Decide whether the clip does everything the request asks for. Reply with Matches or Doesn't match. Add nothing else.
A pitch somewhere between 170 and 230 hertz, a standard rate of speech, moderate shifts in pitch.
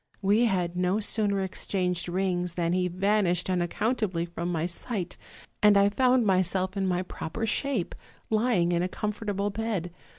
Matches